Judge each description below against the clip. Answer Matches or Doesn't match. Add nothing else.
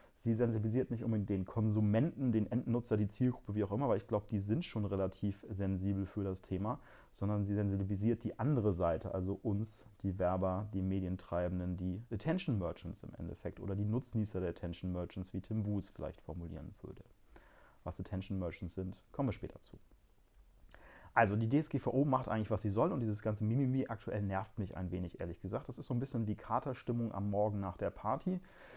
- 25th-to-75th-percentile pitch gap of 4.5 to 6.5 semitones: Doesn't match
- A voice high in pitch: Doesn't match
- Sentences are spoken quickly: Matches